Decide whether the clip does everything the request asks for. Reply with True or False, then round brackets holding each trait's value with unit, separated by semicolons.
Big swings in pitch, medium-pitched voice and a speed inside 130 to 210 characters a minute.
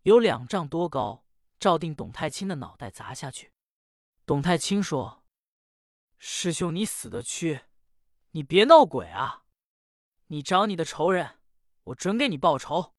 True (7.8 semitones; 165 Hz; 200 characters per minute)